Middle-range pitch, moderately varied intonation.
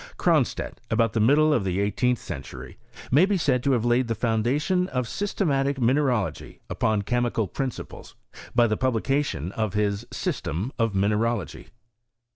No: low, 120 Hz; average, 4.4 semitones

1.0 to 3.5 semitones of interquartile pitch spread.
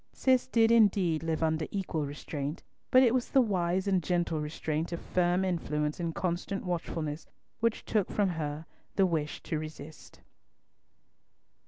No: average, 3.9 semitones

